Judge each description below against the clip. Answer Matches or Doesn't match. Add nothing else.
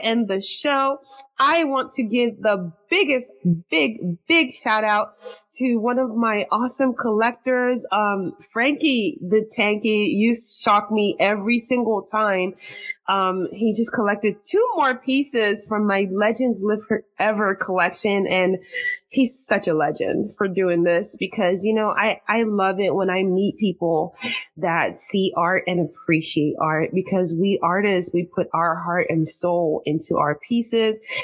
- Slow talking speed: Doesn't match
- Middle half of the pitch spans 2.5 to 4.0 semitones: Doesn't match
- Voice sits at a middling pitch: Doesn't match